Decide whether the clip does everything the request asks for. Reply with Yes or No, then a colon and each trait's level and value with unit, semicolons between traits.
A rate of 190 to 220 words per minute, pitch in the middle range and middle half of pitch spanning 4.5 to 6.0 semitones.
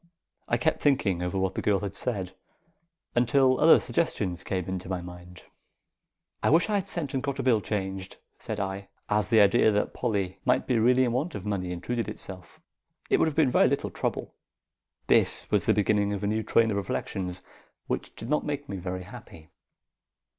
No: average, 195 wpm; low, 105 Hz; average, 5.2 semitones